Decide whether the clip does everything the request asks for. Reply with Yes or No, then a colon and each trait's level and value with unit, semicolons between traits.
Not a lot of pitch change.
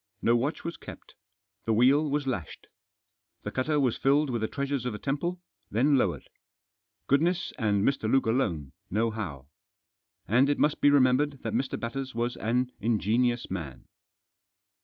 No: average, 4.0 semitones